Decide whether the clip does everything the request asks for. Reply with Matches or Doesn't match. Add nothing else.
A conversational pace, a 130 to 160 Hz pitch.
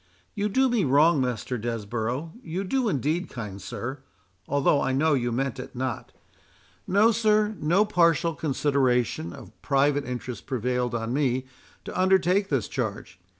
Doesn't match